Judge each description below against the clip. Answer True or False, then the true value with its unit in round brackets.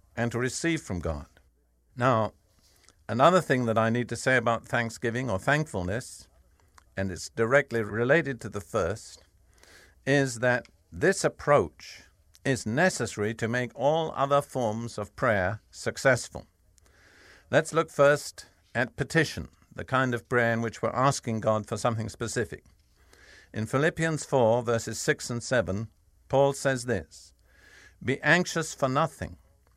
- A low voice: True (115 Hz)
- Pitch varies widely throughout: True (6.3 semitones)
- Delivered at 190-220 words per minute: False (140 wpm)